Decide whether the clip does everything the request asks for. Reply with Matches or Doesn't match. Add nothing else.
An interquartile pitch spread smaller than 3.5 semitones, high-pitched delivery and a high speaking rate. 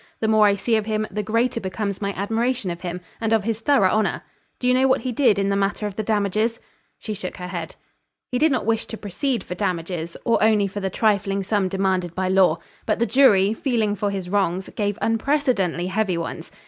Matches